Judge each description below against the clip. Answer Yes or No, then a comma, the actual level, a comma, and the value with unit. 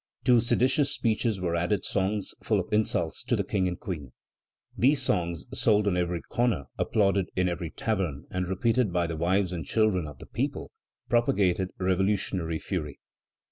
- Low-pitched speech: Yes, very low, 95 Hz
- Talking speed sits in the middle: Yes, average, 165 wpm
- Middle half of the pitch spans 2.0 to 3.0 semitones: No, average, 3.8 semitones